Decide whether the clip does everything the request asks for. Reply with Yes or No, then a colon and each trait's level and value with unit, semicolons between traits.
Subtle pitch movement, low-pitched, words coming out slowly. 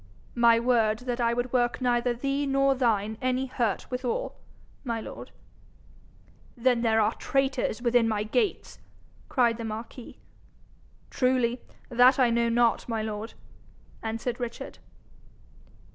No: narrow, 1.8 semitones; high, 240 Hz; slow, 130 wpm